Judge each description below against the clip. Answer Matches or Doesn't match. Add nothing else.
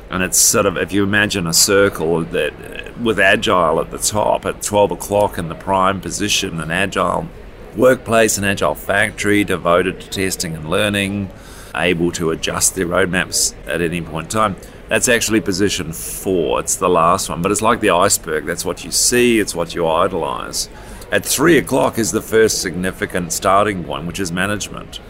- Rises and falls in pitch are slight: Doesn't match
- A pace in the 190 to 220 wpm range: Doesn't match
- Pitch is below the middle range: Matches